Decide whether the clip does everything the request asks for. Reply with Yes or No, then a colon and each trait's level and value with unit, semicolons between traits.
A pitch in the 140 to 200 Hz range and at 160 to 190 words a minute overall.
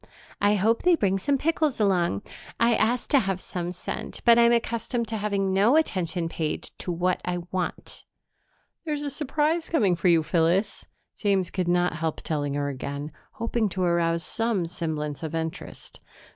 Yes: high, 190 Hz; average, 170 wpm